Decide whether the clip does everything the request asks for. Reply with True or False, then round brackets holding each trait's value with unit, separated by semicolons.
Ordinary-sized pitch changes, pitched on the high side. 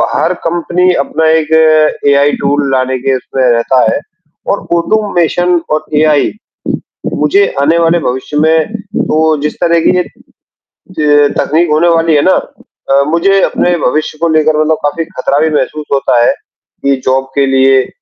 False (3.3 semitones; 155 Hz)